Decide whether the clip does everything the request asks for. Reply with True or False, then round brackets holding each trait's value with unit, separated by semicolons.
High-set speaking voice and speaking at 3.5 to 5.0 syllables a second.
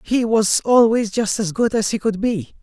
True (215 Hz; 4.5 syllables/s)